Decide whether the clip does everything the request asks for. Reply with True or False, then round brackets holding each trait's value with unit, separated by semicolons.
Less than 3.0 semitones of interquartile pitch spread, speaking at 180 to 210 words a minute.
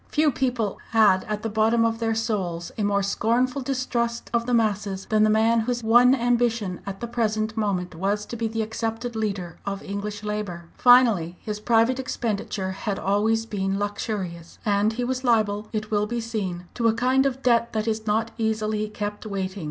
True (2.4 semitones; 190 wpm)